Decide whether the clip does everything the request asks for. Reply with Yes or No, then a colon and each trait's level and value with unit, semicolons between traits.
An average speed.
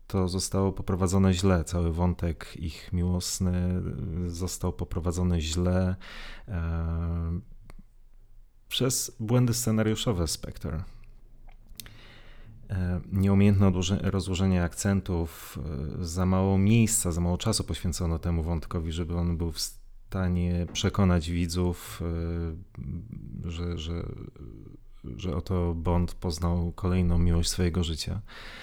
No: slow, 105 wpm